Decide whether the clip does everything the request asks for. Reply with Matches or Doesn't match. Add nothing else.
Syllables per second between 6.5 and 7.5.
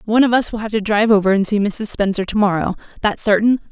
Matches